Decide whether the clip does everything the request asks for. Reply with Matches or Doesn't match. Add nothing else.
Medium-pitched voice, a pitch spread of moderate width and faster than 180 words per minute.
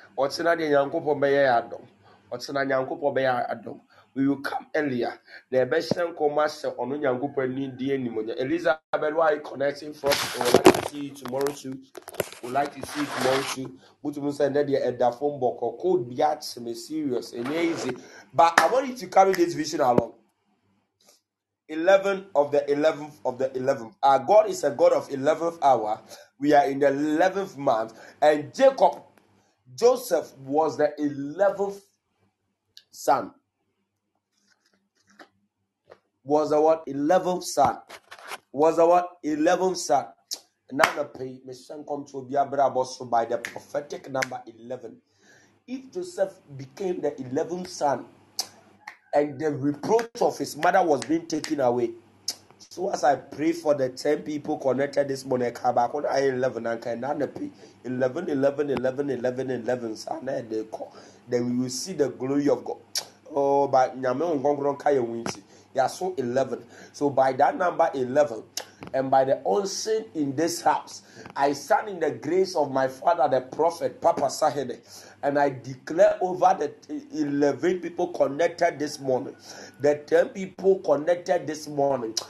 Doesn't match